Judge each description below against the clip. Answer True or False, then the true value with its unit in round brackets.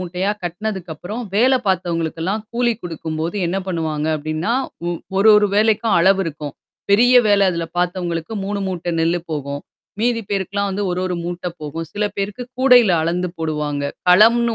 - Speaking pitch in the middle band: True (180 Hz)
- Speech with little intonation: False (4.0 semitones)